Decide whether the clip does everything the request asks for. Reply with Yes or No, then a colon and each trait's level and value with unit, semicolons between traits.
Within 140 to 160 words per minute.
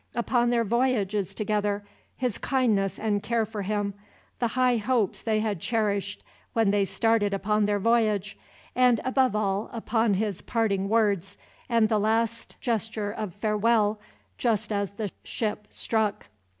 Yes: average, 145 wpm